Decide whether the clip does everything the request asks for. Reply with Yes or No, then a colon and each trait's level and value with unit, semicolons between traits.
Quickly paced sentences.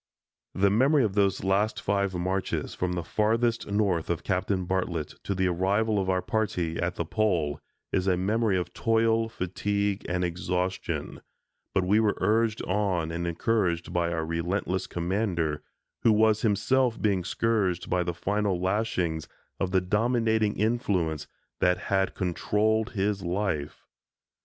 No: average, 145 wpm